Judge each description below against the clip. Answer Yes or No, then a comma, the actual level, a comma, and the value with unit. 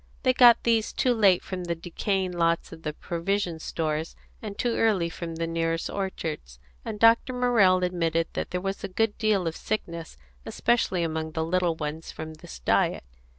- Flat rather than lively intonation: No, average, 3.9 semitones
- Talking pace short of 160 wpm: No, average, 180 wpm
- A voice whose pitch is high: No, medium, 175 Hz